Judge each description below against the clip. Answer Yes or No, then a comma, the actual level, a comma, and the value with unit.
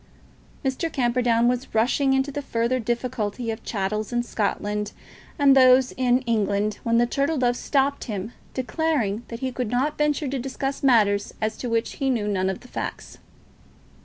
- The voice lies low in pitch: No, high, 245 Hz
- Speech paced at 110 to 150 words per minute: No, average, 175 wpm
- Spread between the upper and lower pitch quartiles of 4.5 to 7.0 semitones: No, average, 3.4 semitones